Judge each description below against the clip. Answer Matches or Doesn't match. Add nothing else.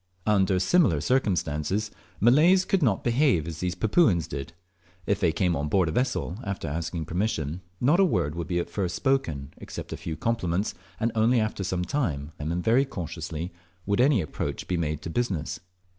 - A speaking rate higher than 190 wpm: Doesn't match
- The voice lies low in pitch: Matches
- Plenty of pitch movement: Matches